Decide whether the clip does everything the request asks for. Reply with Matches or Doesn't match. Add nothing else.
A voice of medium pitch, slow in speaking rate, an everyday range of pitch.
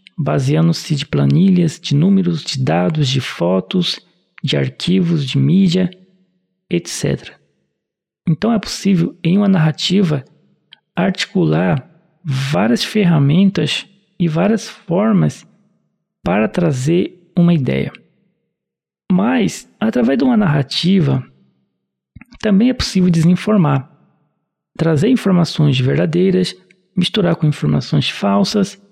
Matches